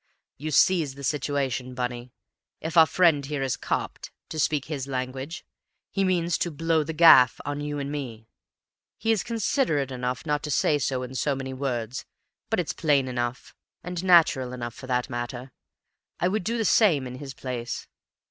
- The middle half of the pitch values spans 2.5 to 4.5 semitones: Yes, average, 4.1 semitones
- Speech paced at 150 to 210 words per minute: Yes, average, 180 wpm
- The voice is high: No, medium, 140 Hz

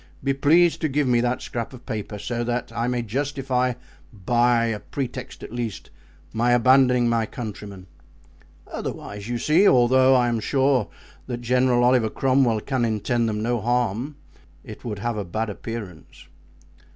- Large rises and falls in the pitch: No, narrow, 2.4 semitones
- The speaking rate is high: No, average, 160 wpm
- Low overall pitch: Yes, low, 120 Hz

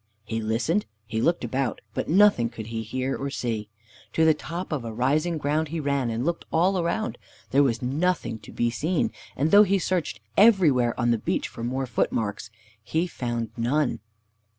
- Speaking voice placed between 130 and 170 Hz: Yes, low, 135 Hz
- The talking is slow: No, average, 185 wpm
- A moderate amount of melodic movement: No, wide, 6.2 semitones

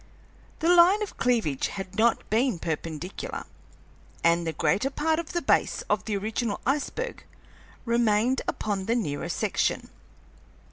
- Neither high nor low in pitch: No, high, 225 Hz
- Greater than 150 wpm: No, slow, 135 wpm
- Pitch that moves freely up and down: Yes, wide, 6.5 semitones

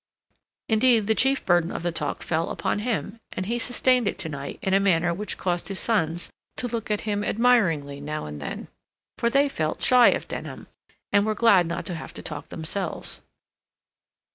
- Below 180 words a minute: No, average, 190 wpm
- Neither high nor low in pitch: No, high, 195 Hz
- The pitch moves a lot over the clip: Yes, wide, 5.8 semitones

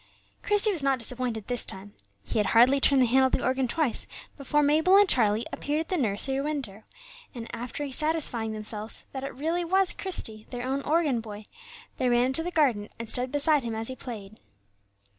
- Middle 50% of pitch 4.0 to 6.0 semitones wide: Yes, average, 4.8 semitones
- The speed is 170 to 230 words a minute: Yes, average, 200 wpm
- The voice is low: No, very high, 260 Hz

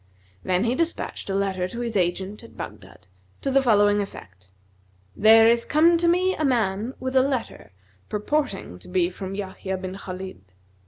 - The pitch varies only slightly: No, wide, 5.5 semitones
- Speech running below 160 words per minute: No, average, 170 wpm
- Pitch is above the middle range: Yes, high, 205 Hz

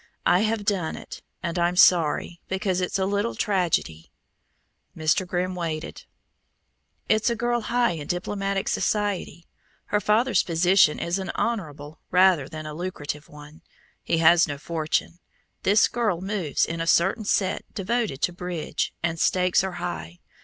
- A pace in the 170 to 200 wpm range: No, average, 150 wpm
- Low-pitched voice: No, medium, 180 Hz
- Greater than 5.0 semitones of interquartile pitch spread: No, average, 3.8 semitones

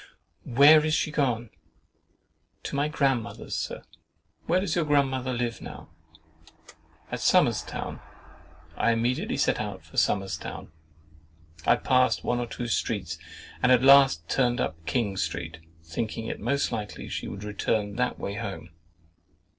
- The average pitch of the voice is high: No, low, 115 Hz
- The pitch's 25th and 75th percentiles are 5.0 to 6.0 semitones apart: Yes, wide, 5.6 semitones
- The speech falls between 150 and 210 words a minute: No, average, 140 wpm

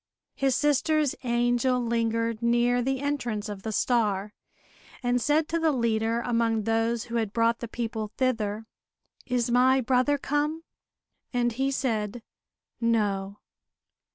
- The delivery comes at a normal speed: No, slow, 130 wpm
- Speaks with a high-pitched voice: Yes, high, 235 Hz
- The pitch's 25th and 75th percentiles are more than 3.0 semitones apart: No, narrow, 2.5 semitones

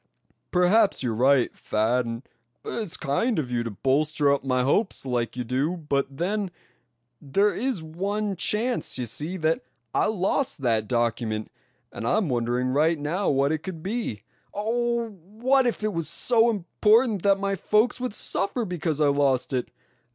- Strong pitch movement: Yes, wide, 8.4 semitones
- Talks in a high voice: No, medium, 160 Hz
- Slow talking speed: No, average, 165 wpm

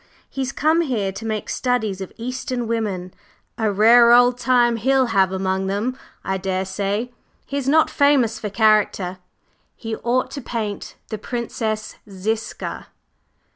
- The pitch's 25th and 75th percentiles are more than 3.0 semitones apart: Yes, average, 3.9 semitones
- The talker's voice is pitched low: No, high, 225 Hz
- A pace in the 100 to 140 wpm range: Yes, slow, 135 wpm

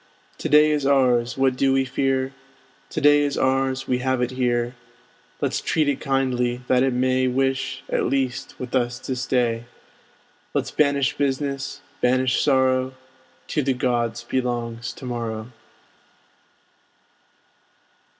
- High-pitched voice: No, low, 130 Hz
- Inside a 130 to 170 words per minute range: Yes, slow, 135 wpm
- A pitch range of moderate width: No, narrow, 1.6 semitones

